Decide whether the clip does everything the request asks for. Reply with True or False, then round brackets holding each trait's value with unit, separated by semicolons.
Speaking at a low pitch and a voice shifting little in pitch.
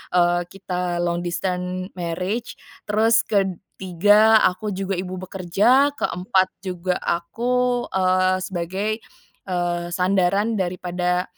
False (185 Hz; 2.2 semitones)